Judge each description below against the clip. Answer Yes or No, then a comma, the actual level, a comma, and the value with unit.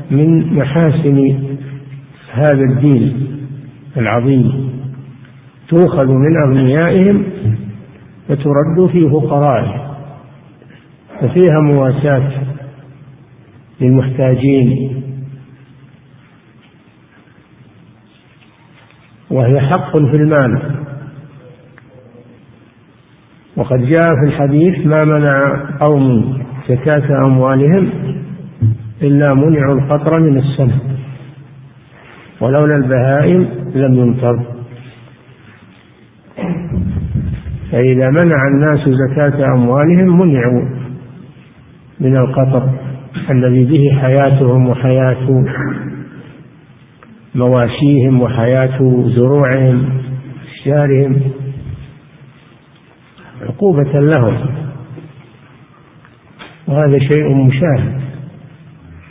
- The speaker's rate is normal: No, slow, 60 wpm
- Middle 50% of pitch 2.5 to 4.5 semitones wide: No, narrow, 2.1 semitones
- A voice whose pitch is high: No, low, 135 Hz